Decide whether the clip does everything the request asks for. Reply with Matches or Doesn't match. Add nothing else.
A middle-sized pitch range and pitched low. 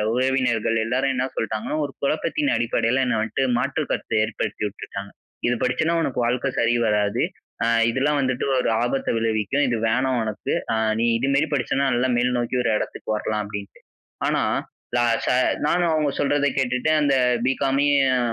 Matches